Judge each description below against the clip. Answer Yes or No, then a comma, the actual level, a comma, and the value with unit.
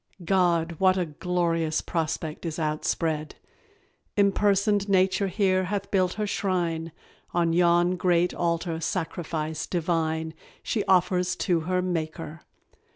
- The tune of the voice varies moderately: No, narrow, 2.3 semitones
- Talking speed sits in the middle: No, slow, 115 wpm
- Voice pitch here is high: No, medium, 175 Hz